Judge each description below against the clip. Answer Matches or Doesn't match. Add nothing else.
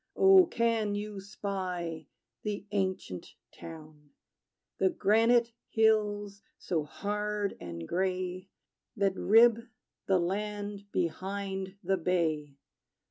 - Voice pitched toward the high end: Matches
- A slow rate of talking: Matches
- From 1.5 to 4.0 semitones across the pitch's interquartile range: Matches